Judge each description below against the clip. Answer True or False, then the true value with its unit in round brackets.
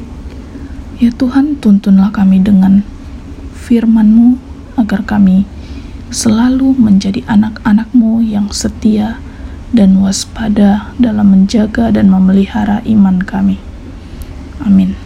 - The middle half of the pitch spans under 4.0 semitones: True (2.8 semitones)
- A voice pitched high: True (210 Hz)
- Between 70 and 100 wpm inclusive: True (90 wpm)